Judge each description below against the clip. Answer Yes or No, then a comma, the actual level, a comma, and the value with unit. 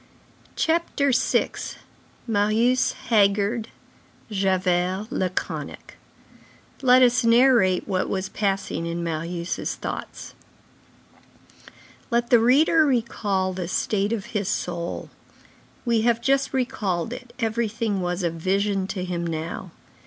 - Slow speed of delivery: Yes, slow, 105 wpm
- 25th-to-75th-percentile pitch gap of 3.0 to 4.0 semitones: No, average, 4.5 semitones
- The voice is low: No, high, 205 Hz